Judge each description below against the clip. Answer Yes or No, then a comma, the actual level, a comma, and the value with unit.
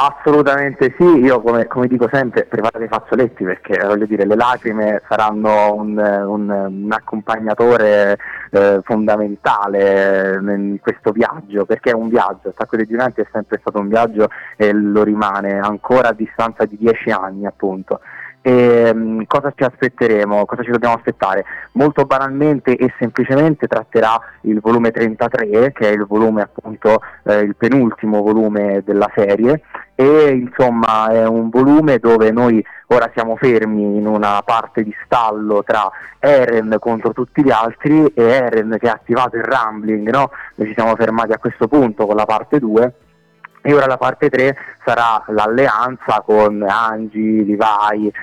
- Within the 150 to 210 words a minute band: Yes, average, 155 wpm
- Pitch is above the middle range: No, low, 110 Hz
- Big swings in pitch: No, narrow, 2.6 semitones